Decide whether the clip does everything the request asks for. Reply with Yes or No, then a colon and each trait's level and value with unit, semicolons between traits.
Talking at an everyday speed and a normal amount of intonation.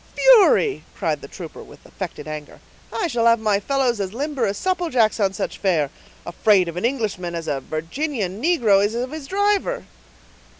No: average, 180 wpm; wide, 8.1 semitones